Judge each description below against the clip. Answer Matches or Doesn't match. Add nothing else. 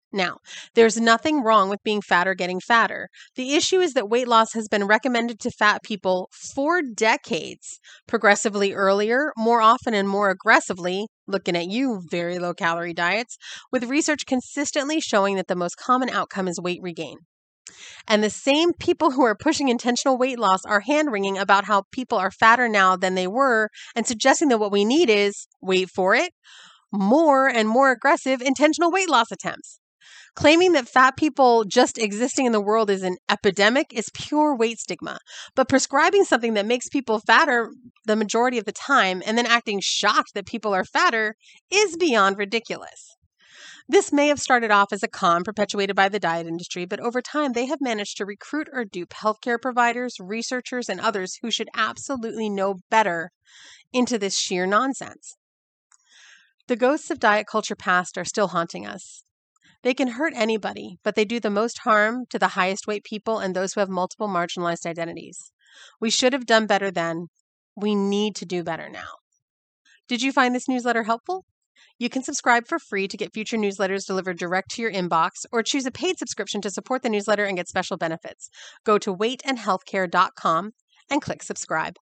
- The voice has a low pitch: Doesn't match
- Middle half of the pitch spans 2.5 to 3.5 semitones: Doesn't match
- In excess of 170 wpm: Matches